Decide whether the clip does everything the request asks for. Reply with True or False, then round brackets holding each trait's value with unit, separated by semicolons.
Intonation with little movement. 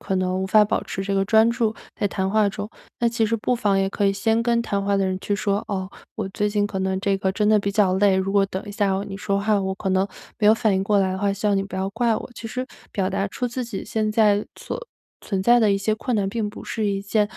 True (2.0 semitones)